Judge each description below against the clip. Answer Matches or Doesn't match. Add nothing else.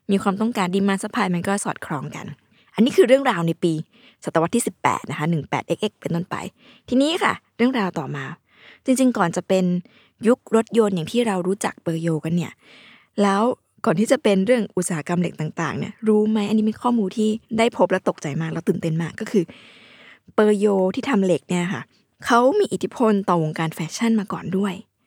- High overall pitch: Matches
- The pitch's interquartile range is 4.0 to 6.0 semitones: Matches